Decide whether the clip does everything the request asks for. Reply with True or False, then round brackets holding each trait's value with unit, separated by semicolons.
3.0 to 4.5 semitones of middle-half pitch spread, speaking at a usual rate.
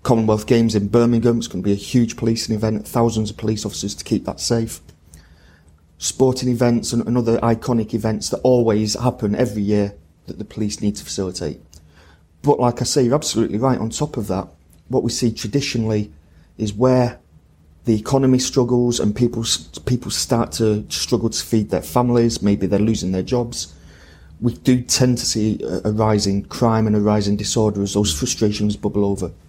True (3.8 semitones; 175 wpm)